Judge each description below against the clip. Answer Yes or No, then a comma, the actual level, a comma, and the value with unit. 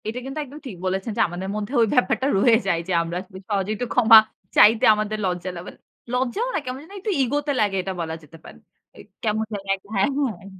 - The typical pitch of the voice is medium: No, high, 215 Hz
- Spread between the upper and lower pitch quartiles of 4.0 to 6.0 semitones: Yes, average, 4.7 semitones